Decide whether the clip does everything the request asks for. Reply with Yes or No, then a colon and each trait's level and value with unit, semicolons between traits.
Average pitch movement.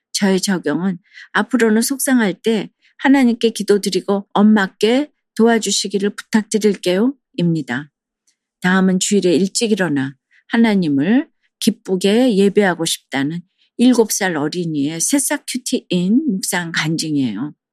Yes: average, 4.3 semitones